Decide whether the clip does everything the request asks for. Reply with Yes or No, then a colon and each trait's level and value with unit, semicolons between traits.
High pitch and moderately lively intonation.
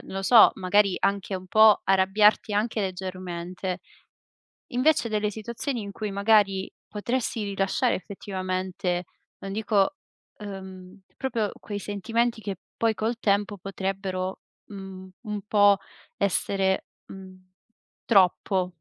No: high, 200 Hz; narrow, 2.1 semitones